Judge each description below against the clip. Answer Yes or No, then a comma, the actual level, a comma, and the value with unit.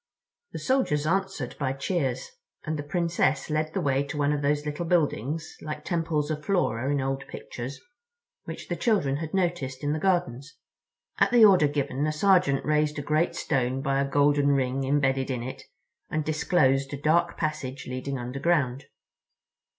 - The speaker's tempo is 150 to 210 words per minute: Yes, average, 170 wpm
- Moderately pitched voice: Yes, medium, 145 Hz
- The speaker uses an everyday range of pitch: Yes, average, 3.0 semitones